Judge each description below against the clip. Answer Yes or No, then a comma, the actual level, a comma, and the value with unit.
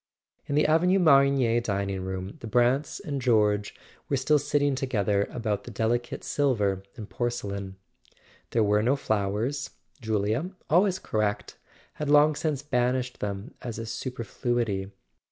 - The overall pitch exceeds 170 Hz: No, low, 120 Hz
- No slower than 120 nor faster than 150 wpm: Yes, average, 145 wpm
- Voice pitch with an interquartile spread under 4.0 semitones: No, average, 5.2 semitones